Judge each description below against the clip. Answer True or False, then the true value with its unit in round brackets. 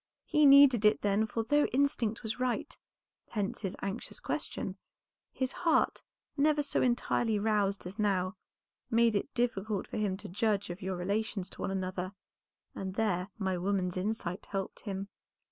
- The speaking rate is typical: True (160 wpm)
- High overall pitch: True (210 Hz)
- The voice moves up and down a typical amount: True (3.5 semitones)